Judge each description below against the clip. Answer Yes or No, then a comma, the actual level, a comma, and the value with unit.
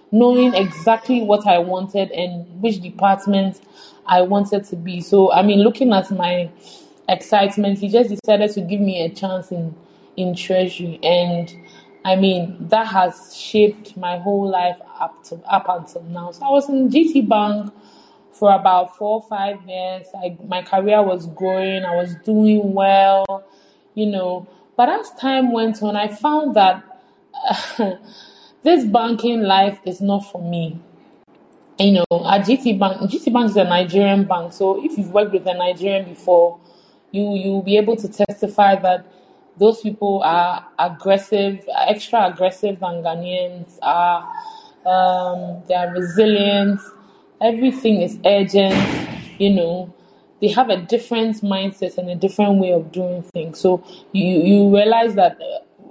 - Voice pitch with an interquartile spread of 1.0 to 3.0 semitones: Yes, average, 2.7 semitones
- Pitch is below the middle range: No, high, 195 Hz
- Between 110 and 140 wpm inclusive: No, average, 155 wpm